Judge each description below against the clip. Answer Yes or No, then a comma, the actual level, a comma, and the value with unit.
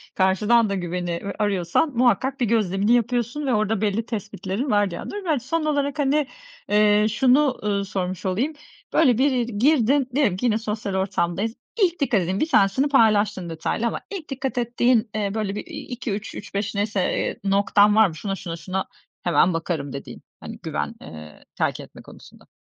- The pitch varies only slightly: No, average, 4.6 semitones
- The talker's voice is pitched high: Yes, high, 215 Hz